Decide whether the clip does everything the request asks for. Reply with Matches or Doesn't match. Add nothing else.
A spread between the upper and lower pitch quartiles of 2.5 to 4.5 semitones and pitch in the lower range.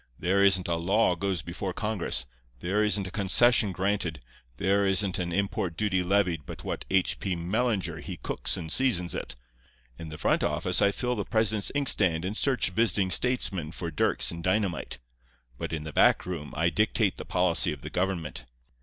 Matches